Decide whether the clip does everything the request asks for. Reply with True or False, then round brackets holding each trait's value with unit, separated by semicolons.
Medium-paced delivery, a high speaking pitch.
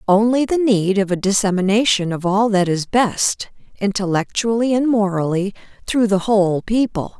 True (150 wpm; 205 Hz)